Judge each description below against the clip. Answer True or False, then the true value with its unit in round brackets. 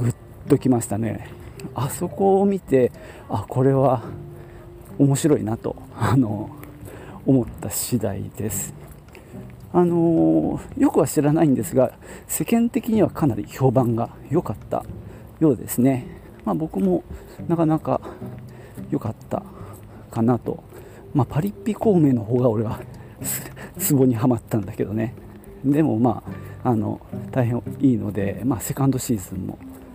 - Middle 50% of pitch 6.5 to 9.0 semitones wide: False (5.4 semitones)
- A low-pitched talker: True (125 Hz)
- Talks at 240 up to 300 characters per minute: True (250 characters per minute)